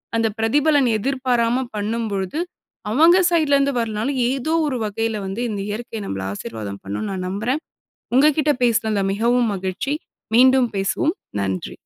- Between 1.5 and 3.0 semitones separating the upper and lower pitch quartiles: No, average, 5.0 semitones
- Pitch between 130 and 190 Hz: No, high, 230 Hz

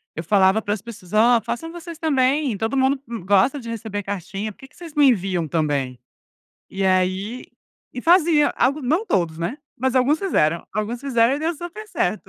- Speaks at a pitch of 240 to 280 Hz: No, high, 230 Hz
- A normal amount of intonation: No, wide, 6.7 semitones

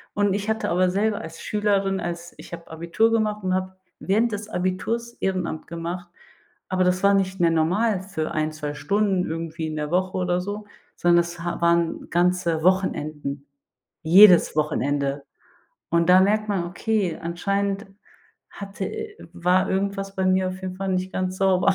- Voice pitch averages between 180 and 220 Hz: Yes, medium, 185 Hz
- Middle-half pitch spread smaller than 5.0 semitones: Yes, average, 2.7 semitones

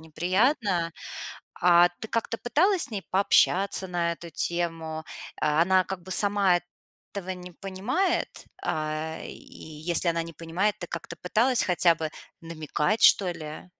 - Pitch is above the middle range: No, medium, 180 Hz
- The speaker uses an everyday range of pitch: Yes, average, 3.3 semitones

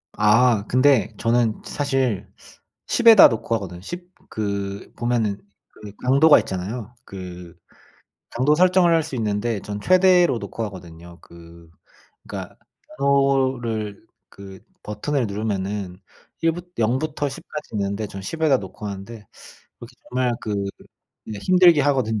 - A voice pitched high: No, low, 115 Hz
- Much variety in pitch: Yes, wide, 5.7 semitones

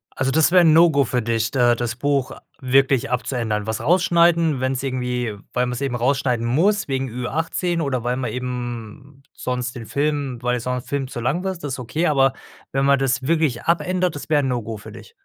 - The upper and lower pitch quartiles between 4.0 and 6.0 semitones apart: No, average, 3.2 semitones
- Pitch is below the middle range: Yes, low, 130 Hz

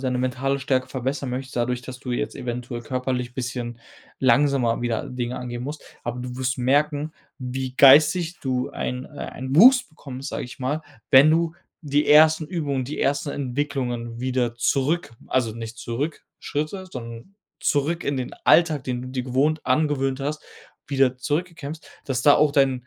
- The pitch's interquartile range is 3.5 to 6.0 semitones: No, average, 2.9 semitones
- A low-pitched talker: Yes, low, 130 Hz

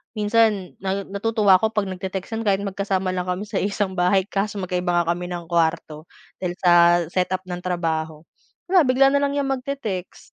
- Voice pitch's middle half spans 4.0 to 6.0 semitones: No, average, 3.0 semitones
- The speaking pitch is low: No, high, 190 Hz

